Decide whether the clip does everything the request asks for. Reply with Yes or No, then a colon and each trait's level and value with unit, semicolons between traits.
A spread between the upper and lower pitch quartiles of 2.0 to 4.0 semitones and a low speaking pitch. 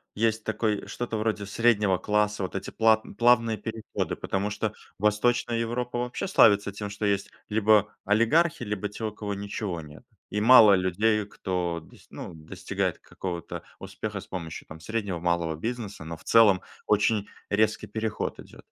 Yes: average, 2.7 semitones; low, 105 Hz